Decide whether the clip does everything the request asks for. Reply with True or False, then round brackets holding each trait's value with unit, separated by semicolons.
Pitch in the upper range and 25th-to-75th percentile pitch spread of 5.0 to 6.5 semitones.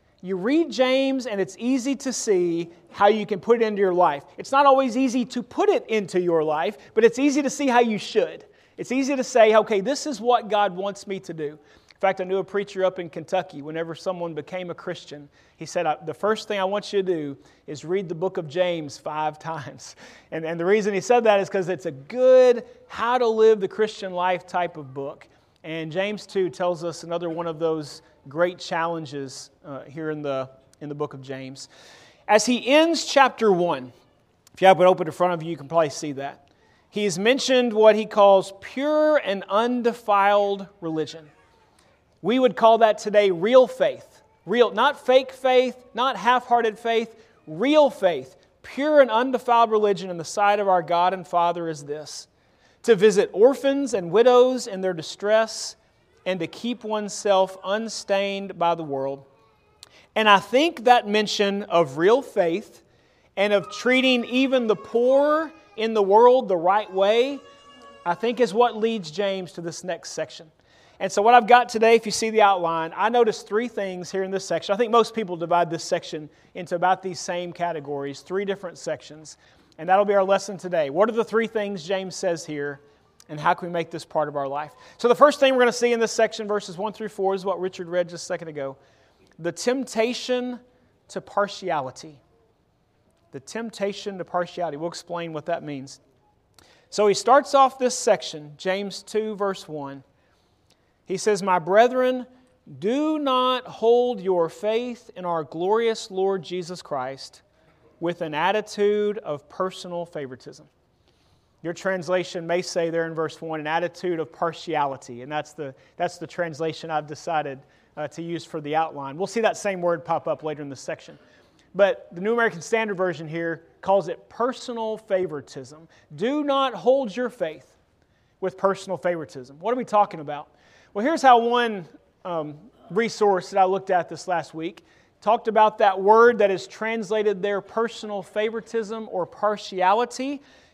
True (195 Hz; 5.5 semitones)